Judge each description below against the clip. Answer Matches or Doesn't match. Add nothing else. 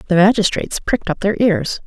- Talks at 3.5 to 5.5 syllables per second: Doesn't match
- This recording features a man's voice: Doesn't match